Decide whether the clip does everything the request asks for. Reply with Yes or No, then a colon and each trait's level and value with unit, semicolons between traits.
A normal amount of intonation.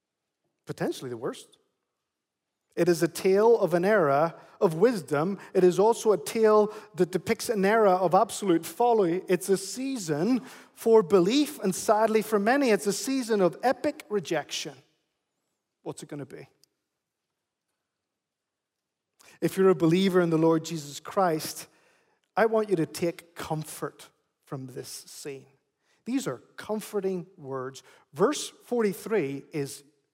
Yes: average, 4.6 semitones